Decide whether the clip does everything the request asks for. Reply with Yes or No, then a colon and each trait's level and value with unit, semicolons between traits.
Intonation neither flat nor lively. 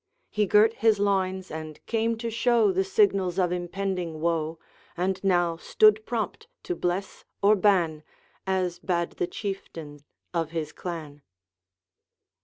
Yes: average, 3.5 semitones